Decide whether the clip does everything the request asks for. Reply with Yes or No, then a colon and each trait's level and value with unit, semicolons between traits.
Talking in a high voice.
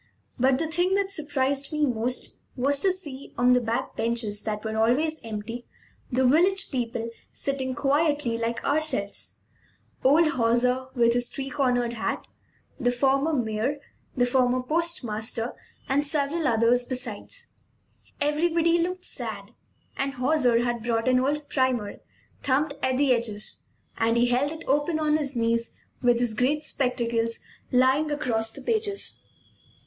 Yes: very high, 260 Hz